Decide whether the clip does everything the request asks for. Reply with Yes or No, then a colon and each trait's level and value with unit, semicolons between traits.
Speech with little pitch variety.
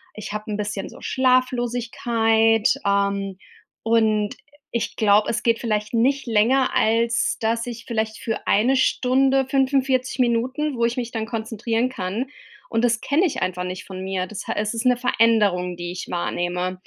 No: average, 3.1 semitones